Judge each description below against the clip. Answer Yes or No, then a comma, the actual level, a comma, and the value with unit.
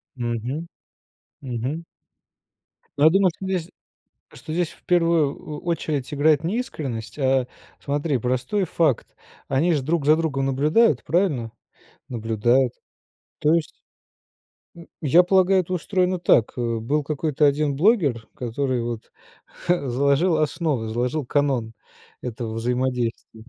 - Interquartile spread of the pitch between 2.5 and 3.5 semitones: No, average, 5.1 semitones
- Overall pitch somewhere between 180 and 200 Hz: No, medium, 145 Hz